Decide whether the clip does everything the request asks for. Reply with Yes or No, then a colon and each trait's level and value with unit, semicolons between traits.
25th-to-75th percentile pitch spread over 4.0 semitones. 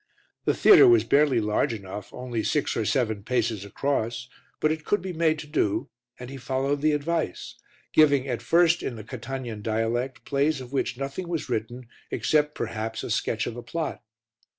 Yes: average, 4.8 semitones